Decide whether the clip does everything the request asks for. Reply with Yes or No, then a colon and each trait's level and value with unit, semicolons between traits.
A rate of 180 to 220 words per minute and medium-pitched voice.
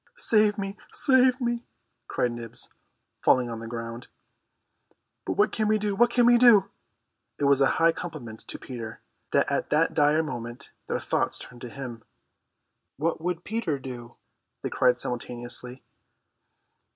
No: average, 150 wpm; medium, 145 Hz